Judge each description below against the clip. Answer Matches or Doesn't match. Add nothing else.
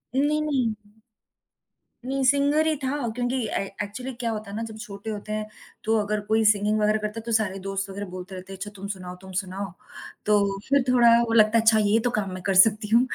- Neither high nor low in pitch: Doesn't match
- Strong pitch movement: Doesn't match